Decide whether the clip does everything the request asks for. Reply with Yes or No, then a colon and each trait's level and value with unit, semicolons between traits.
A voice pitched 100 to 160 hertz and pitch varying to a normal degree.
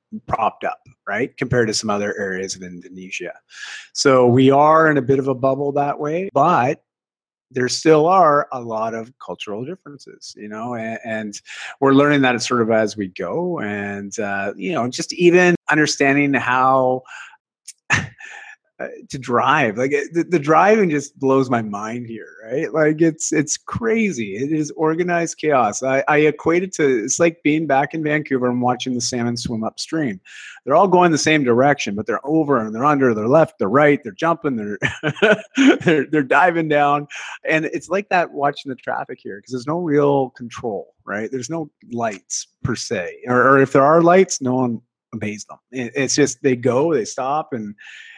Yes: medium, 140 Hz; average, 4.6 semitones